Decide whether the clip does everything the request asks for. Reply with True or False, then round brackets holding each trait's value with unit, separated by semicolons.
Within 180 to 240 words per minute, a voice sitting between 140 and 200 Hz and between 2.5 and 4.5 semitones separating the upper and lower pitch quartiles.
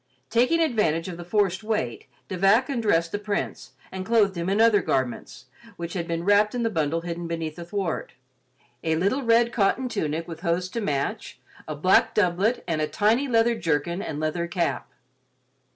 False (185 wpm; 185 Hz; 4.9 semitones)